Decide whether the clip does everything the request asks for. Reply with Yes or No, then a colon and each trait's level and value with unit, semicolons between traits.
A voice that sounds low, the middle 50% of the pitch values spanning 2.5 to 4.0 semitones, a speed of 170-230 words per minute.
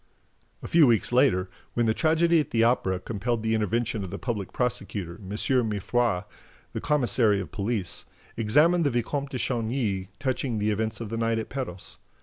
Yes: low, 115 Hz; average, 3.6 semitones; average, 175 wpm